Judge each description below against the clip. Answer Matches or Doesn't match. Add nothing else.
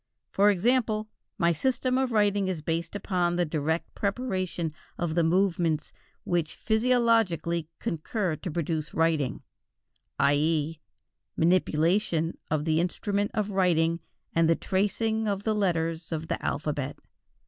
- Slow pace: Matches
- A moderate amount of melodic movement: Matches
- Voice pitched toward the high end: Doesn't match